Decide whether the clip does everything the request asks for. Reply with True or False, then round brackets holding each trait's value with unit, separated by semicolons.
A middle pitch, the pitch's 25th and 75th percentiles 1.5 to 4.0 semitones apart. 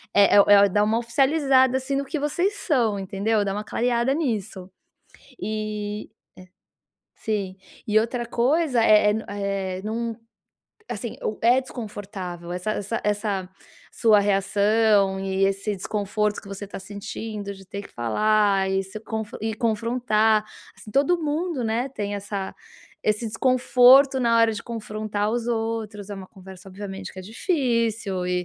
False (215 Hz; 2.9 semitones)